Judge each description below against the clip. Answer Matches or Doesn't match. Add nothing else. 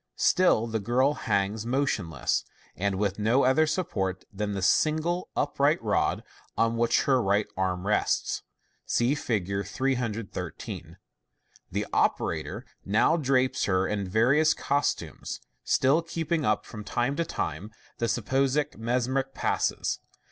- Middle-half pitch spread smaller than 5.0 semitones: Doesn't match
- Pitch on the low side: Matches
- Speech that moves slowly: Matches